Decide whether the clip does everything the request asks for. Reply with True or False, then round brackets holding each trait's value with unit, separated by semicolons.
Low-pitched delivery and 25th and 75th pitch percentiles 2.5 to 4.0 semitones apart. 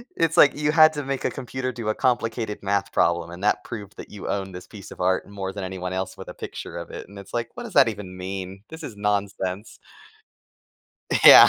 False (105 Hz; 5.2 semitones)